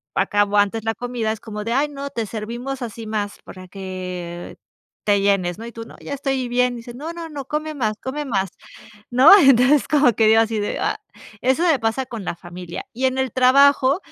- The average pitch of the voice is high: Yes, high, 235 Hz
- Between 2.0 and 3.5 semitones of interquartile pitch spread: No, average, 4.6 semitones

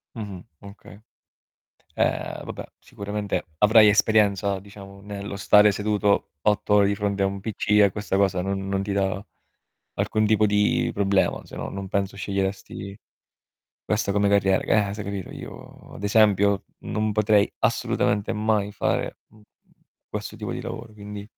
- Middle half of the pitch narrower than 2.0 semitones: Yes, narrow, 1.1 semitones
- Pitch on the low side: Yes, low, 100 Hz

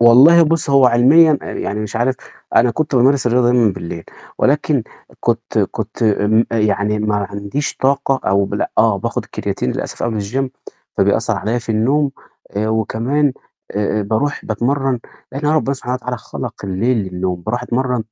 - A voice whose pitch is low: Yes, low, 120 Hz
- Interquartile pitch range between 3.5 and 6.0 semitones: Yes, average, 4.2 semitones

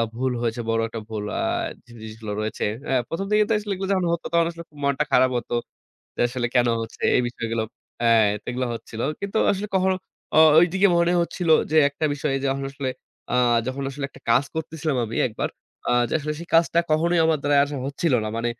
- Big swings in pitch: Yes, wide, 6.2 semitones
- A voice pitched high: No, medium, 140 Hz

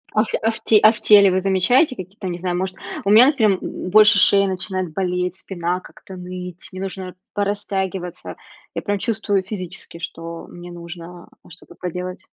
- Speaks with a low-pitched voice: No, medium, 185 Hz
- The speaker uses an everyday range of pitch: No, narrow, 2.1 semitones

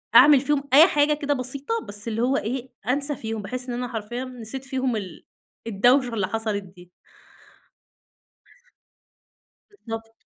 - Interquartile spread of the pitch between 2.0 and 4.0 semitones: Yes, average, 3.5 semitones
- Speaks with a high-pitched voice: Yes, very high, 250 Hz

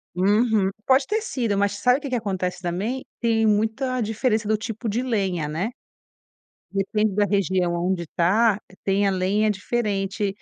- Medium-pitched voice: No, high, 205 Hz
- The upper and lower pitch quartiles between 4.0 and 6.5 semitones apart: No, average, 3.1 semitones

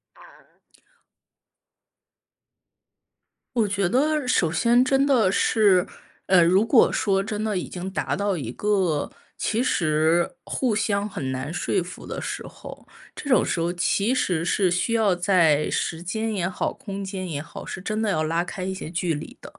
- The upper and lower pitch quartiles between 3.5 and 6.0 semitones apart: Yes, average, 4.0 semitones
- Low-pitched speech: No, high, 190 Hz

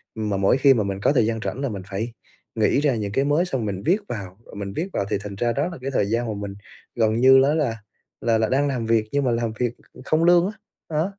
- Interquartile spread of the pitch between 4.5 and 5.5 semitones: Yes, average, 4.8 semitones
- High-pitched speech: No, low, 120 Hz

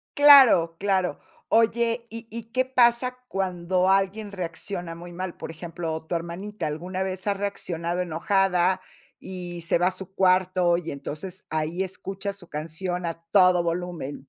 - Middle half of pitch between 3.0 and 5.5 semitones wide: No, narrow, 2.5 semitones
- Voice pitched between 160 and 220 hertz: Yes, medium, 185 Hz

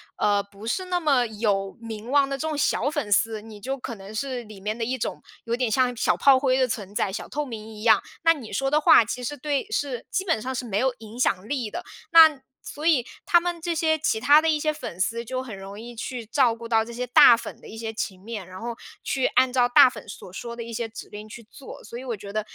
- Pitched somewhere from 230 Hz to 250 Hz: Yes, high, 235 Hz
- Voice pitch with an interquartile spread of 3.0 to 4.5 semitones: Yes, average, 4.1 semitones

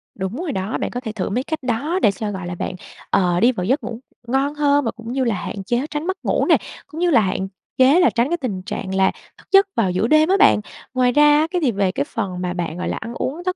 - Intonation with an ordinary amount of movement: No, wide, 7.5 semitones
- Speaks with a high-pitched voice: Yes, high, 240 Hz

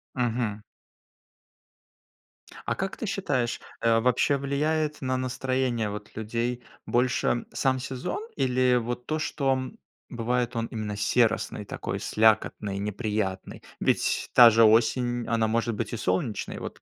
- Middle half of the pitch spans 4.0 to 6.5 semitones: No, average, 2.7 semitones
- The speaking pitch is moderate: No, low, 120 Hz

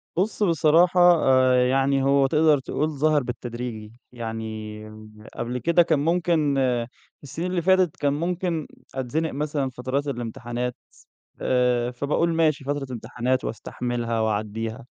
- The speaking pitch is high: No, low, 135 Hz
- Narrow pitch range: No, average, 4.5 semitones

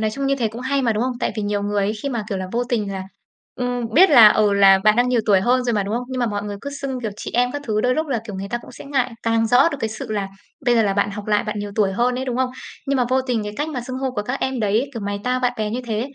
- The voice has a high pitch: Yes, high, 235 Hz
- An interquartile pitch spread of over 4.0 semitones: No, average, 3.4 semitones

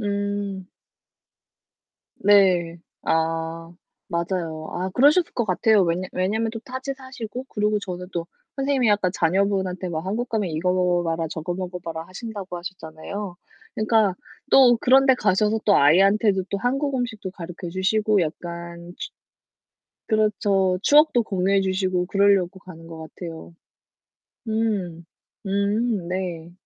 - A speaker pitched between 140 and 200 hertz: Yes, high, 190 Hz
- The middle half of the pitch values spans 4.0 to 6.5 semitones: No, average, 3.6 semitones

